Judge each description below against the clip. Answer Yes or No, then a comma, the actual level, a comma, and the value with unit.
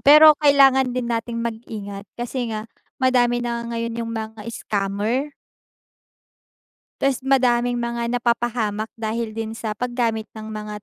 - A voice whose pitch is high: Yes, high, 235 Hz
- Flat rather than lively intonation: Yes, narrow, 2.1 semitones